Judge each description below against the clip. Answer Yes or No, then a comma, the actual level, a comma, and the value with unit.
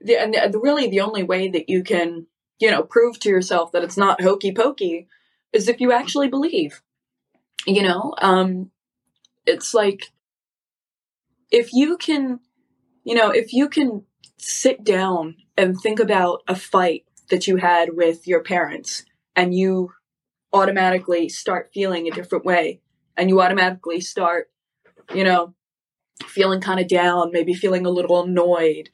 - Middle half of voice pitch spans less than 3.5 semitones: No, average, 4.4 semitones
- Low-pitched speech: No, high, 190 Hz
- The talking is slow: No, average, 150 wpm